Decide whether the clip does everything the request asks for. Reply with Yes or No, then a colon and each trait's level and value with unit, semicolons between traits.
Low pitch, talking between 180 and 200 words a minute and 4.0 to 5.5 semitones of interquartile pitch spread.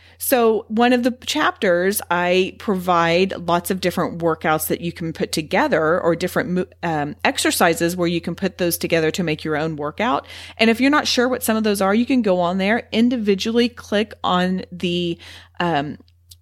No: medium, 180 Hz; average, 185 wpm; average, 4.9 semitones